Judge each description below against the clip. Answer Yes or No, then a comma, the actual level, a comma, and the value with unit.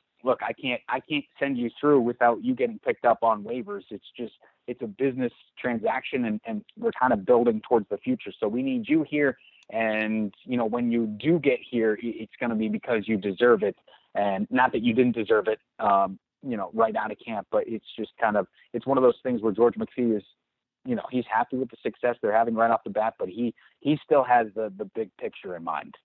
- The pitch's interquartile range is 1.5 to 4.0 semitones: No, average, 4.5 semitones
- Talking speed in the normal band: No, fast, 235 wpm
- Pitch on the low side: Yes, low, 120 Hz